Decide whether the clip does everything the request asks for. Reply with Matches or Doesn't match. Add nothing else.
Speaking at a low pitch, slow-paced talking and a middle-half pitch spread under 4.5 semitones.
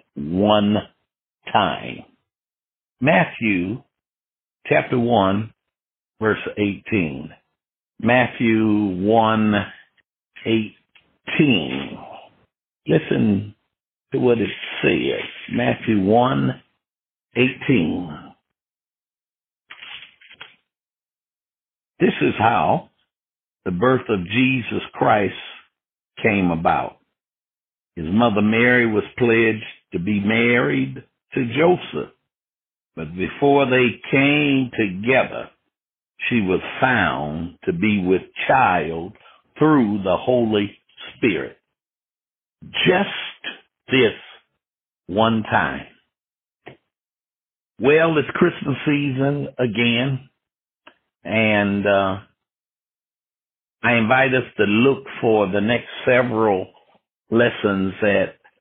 Matches